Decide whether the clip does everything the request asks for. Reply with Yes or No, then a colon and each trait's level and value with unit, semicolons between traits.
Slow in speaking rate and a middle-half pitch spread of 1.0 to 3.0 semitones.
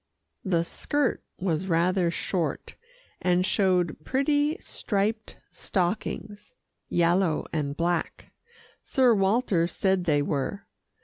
No: slow, 100 wpm; average, 3.7 semitones